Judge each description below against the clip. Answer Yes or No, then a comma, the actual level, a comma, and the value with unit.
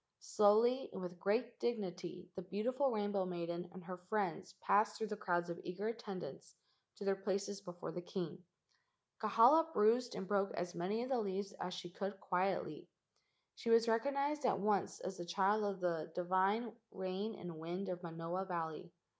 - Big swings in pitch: No, average, 3.3 semitones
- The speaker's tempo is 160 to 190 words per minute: Yes, average, 170 wpm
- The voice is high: Yes, high, 195 Hz